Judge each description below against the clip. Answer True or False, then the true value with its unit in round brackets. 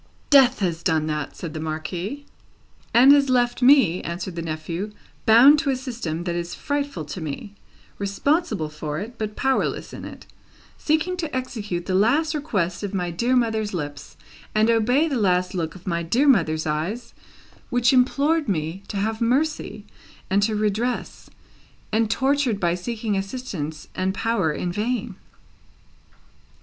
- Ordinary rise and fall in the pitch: False (6.7 semitones)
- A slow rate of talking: False (155 wpm)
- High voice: True (210 Hz)